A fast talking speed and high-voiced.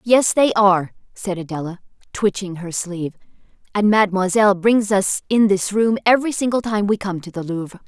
No: average, 175 wpm; high, 200 Hz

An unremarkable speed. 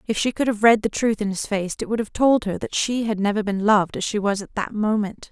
No: fast, 305 wpm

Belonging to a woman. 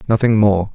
No: male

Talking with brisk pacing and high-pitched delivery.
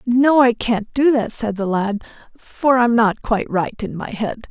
Yes: fast, 215 wpm; high, 230 Hz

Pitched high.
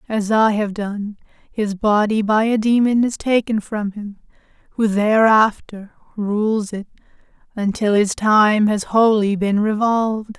Yes: high, 210 Hz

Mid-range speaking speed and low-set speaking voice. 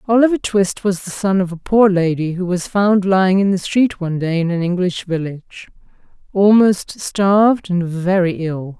No: average, 185 wpm; medium, 185 Hz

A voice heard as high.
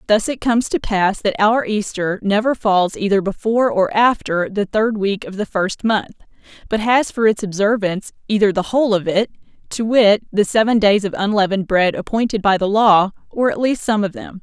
Yes: high, 205 Hz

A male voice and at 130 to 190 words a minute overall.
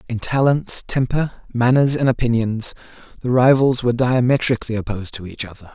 Yes: male; average, 145 wpm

